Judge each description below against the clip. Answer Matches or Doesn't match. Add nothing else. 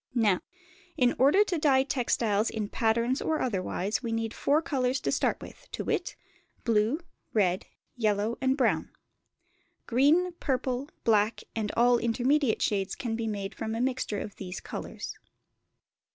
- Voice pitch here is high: Matches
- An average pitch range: Matches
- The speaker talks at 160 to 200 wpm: Doesn't match